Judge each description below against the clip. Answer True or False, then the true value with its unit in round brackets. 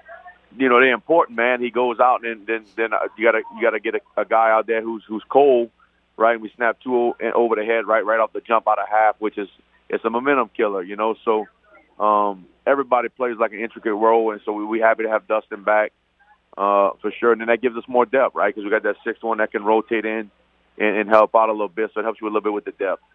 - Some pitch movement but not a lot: False (1.5 semitones)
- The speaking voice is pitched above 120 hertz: False (110 Hz)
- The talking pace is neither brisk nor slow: False (270 wpm)